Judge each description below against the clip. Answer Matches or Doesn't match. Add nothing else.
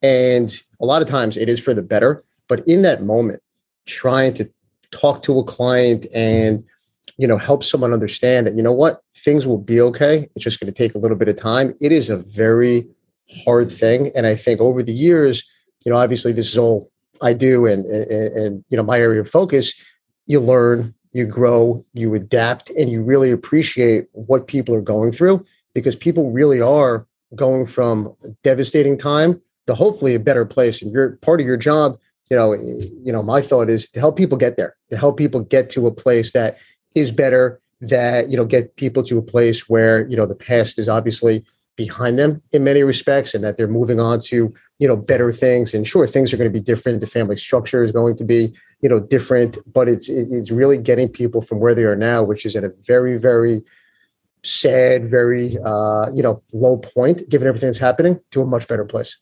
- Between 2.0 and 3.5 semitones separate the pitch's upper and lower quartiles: Matches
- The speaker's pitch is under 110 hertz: Doesn't match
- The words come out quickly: Matches